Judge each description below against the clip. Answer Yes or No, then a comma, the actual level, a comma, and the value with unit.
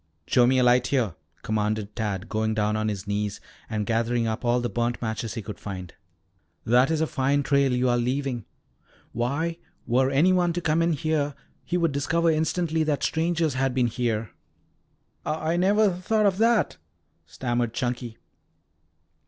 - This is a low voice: Yes, low, 125 Hz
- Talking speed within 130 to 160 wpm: No, average, 170 wpm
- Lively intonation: Yes, wide, 5.9 semitones